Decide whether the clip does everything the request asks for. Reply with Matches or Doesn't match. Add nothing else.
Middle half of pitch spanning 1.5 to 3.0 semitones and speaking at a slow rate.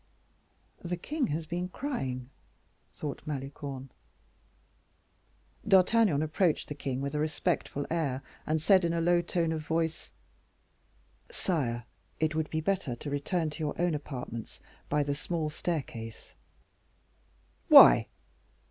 Doesn't match